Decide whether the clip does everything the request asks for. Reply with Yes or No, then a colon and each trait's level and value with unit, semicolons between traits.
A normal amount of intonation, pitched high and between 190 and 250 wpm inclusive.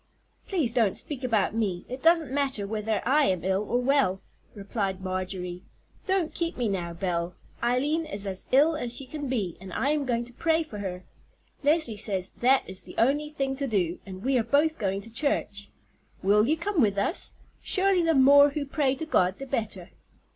No: wide, 6.6 semitones; high, 240 Hz; average, 200 wpm